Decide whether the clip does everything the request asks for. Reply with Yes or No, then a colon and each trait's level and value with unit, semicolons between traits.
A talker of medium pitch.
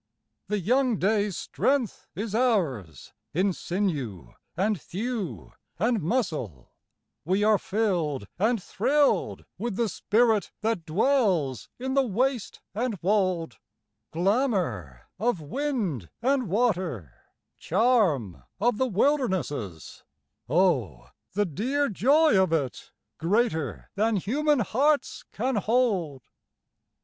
No: high, 205 Hz